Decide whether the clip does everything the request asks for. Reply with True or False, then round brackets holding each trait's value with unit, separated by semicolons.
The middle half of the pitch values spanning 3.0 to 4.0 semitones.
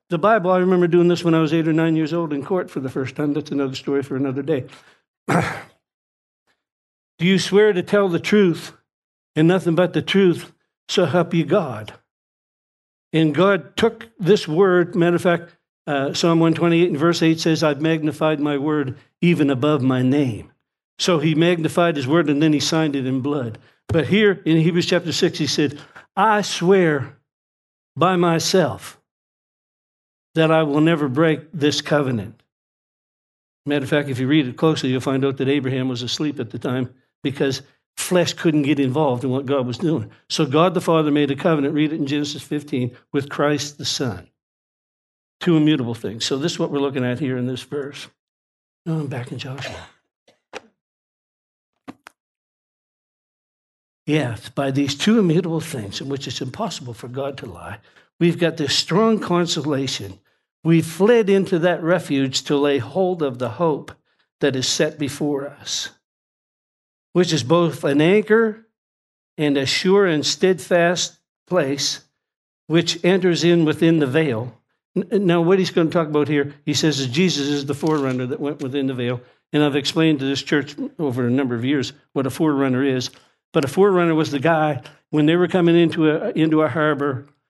True (3.7 semitones)